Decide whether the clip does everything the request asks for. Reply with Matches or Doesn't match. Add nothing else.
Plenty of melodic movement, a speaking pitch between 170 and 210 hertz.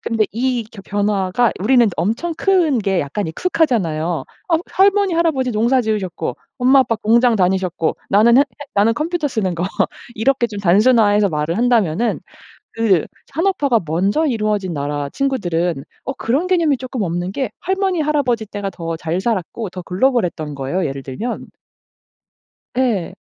Doesn't match